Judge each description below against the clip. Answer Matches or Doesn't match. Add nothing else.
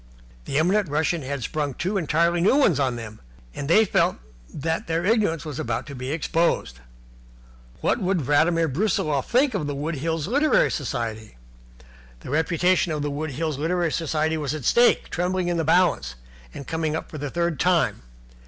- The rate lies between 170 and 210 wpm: Matches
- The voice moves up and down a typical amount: Matches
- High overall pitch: Doesn't match